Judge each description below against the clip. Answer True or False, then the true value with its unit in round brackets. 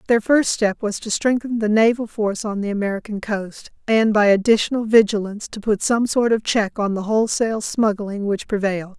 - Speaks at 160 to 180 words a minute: False (195 wpm)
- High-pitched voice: True (215 Hz)